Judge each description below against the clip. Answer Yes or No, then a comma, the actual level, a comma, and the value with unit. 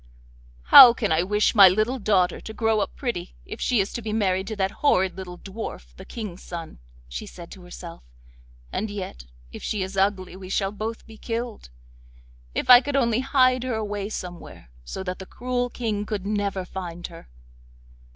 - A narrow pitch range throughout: No, average, 3.5 semitones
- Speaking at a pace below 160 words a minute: No, average, 190 wpm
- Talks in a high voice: Yes, high, 200 Hz